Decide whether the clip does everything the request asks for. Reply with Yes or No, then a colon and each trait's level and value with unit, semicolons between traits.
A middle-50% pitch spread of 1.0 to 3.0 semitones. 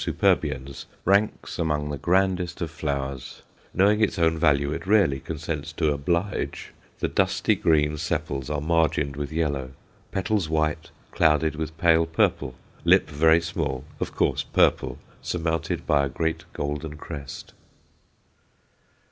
Yes: narrow, 2.5 semitones